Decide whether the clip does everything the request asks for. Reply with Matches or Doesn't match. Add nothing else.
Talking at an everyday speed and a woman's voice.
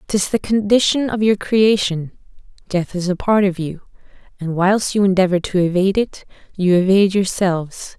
Matches